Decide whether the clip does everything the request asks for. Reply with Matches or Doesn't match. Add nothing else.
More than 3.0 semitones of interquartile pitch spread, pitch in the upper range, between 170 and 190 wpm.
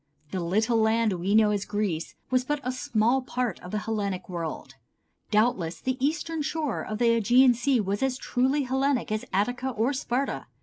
Matches